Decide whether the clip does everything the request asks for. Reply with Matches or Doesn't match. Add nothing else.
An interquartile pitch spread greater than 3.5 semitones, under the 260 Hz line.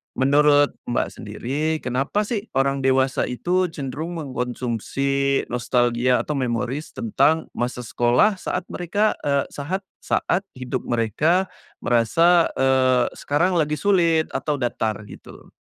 Matches